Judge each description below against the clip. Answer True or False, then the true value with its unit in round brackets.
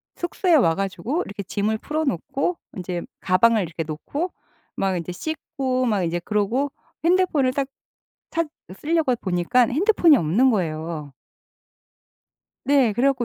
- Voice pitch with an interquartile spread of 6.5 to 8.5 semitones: True (8.1 semitones)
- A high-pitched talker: True (235 Hz)